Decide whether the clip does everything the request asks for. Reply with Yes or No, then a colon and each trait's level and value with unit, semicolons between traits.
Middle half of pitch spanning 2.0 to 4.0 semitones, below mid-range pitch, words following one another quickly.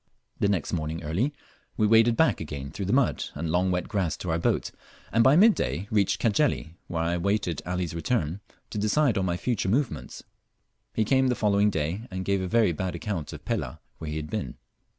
No: average, 5.1 semitones; very low, 95 Hz; fast, 210 wpm